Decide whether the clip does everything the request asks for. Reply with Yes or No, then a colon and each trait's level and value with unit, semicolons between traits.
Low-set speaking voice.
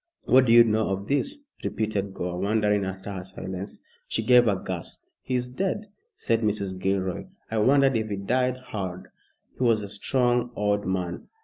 Yes: low, 105 Hz